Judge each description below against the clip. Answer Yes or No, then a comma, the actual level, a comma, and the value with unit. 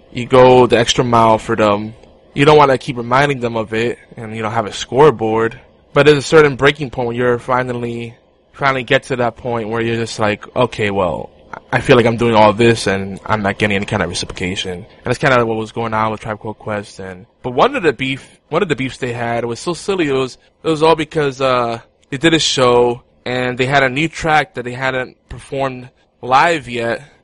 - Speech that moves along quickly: Yes, fast, 240 wpm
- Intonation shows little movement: No, average, 3.2 semitones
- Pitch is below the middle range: Yes, low, 120 Hz